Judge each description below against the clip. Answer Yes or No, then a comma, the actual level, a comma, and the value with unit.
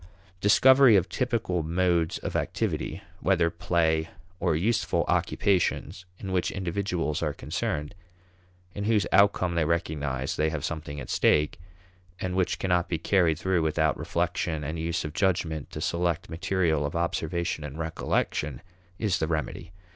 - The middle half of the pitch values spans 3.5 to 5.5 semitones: No, average, 2.9 semitones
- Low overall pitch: Yes, very low, 85 Hz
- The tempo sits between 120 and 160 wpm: Yes, average, 145 wpm